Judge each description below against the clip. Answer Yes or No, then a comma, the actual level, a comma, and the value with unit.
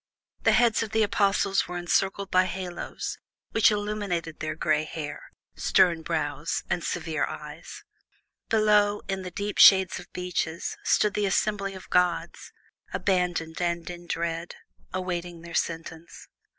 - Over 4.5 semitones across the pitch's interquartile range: No, average, 3.1 semitones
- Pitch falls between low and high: Yes, medium, 180 Hz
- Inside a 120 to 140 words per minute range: Yes, slow, 135 wpm